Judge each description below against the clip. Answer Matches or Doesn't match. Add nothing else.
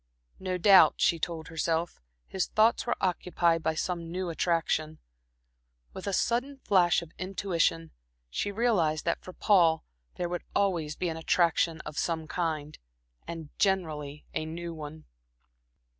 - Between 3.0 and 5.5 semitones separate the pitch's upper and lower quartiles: Doesn't match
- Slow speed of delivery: Doesn't match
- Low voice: Doesn't match